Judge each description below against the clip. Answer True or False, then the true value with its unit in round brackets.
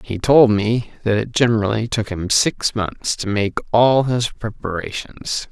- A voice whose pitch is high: False (110 Hz)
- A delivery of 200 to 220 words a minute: False (165 wpm)